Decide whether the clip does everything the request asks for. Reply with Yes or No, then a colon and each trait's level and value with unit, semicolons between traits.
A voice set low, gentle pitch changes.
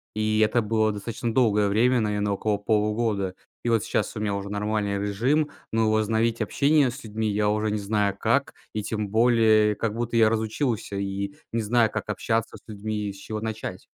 Yes: low, 110 Hz; narrow, 1.6 semitones